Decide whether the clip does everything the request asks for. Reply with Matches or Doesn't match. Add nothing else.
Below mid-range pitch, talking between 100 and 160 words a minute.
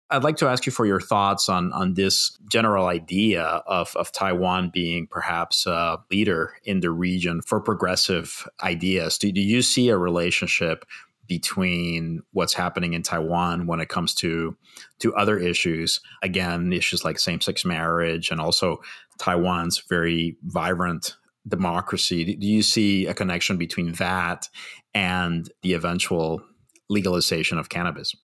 Matches